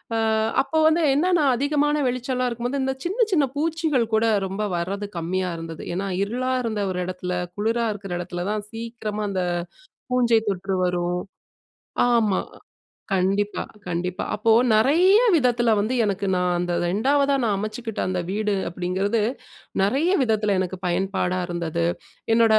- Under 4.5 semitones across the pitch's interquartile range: No, average, 5.3 semitones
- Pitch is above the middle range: Yes, high, 210 Hz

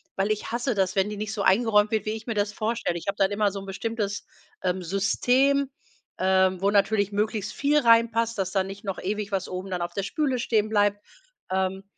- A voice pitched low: No, high, 205 Hz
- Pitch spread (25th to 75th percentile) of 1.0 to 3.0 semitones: Yes, narrow, 2.5 semitones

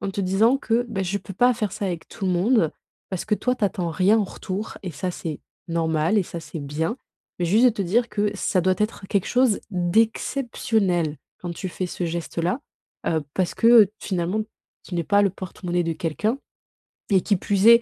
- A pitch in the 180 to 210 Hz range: Yes, high, 190 Hz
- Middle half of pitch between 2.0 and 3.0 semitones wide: No, average, 4.0 semitones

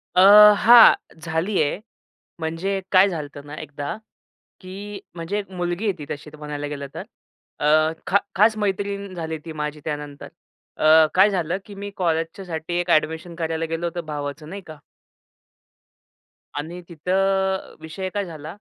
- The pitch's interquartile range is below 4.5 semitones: Yes, average, 3.7 semitones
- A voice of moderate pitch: Yes, medium, 165 Hz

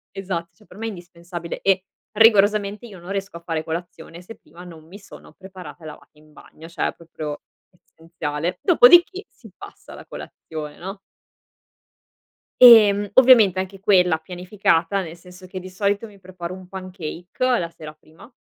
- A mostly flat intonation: No, average, 3.0 semitones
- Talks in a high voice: No, medium, 180 Hz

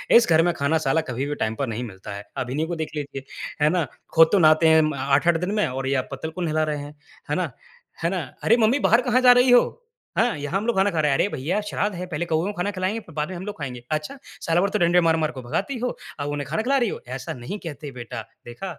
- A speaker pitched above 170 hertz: No, medium, 160 Hz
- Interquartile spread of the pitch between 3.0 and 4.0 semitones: No, wide, 5.5 semitones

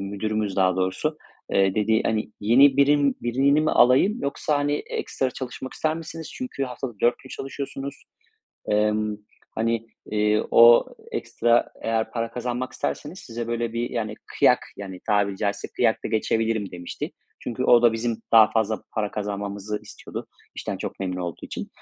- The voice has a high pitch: No, low, 115 Hz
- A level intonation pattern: No, average, 3.6 semitones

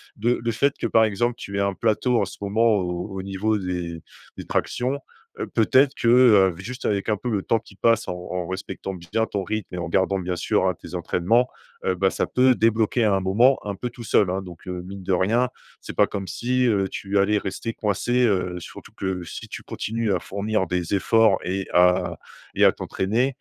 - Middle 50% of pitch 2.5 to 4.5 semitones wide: Yes, average, 3.6 semitones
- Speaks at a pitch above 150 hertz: No, low, 100 Hz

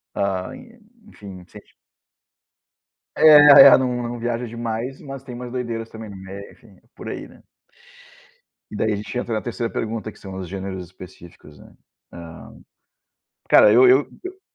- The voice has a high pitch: No, low, 115 Hz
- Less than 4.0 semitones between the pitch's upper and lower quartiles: No, average, 4.4 semitones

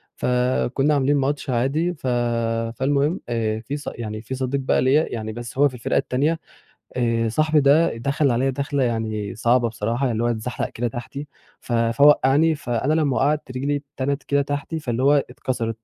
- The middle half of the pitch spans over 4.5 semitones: No, average, 3.4 semitones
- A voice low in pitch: Yes, low, 130 Hz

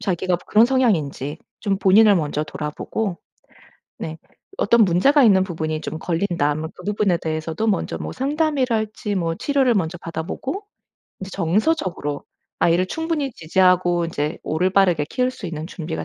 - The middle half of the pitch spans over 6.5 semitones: No, wide, 5.6 semitones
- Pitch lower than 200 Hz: Yes, medium, 185 Hz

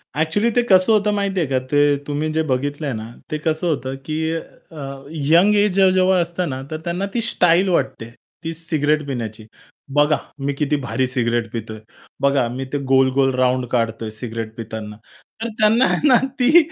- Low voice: No, medium, 145 Hz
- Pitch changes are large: Yes, wide, 5.9 semitones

